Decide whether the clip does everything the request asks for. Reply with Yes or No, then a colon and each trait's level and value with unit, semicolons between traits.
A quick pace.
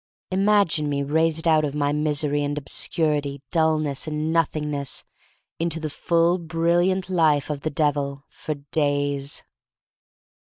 No: slow, 135 wpm